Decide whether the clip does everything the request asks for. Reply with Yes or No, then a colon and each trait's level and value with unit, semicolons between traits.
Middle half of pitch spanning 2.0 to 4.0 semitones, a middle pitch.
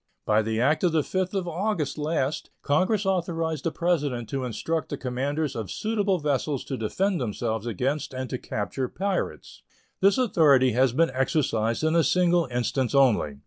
No: wide, 5.4 semitones; medium, 145 Hz